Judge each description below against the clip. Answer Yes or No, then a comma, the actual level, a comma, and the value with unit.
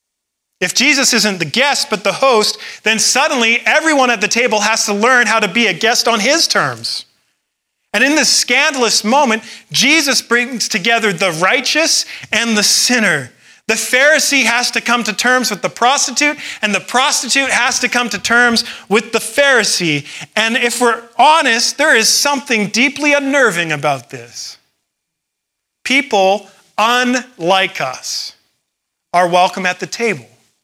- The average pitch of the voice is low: No, high, 230 Hz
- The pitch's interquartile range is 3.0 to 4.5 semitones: Yes, average, 4.1 semitones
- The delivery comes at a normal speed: Yes, average, 155 wpm